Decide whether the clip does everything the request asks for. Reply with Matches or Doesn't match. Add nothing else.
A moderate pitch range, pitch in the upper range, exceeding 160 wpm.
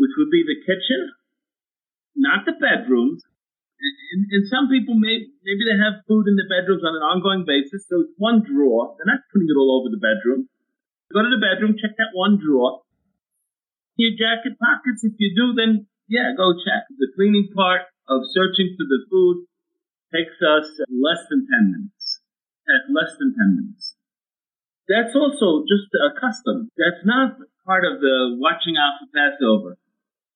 Doesn't match